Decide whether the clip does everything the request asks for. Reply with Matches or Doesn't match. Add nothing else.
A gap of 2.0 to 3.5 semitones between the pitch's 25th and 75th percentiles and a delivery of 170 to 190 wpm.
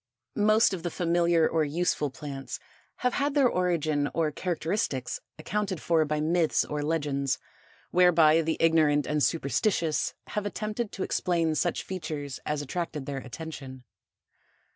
Doesn't match